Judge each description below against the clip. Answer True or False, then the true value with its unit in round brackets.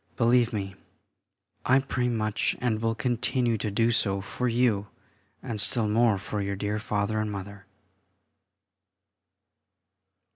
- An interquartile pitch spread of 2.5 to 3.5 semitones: True (2.8 semitones)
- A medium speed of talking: False (125 wpm)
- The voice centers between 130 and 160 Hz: False (110 Hz)